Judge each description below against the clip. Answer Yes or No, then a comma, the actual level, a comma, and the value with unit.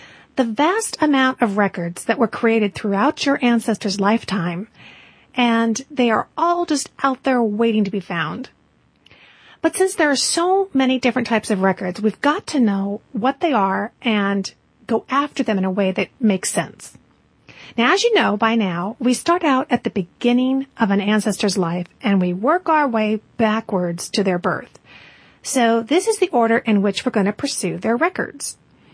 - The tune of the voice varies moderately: Yes, average, 4.9 semitones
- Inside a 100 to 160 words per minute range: No, average, 180 wpm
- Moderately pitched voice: No, high, 230 Hz